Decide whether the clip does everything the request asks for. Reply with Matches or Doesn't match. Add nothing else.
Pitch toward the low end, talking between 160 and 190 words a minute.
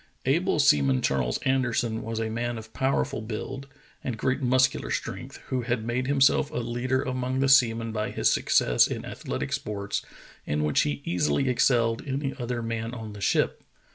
Matches